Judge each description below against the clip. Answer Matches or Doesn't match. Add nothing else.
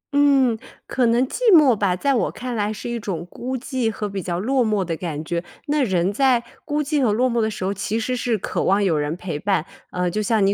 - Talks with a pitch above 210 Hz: Matches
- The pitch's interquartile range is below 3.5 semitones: Doesn't match